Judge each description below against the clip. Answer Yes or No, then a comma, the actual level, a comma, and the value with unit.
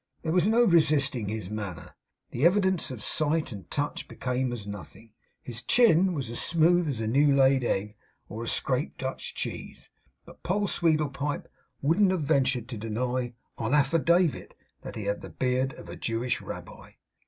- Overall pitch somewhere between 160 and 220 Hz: No, low, 135 Hz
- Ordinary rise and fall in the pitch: No, wide, 5.8 semitones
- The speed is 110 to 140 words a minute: No, average, 170 wpm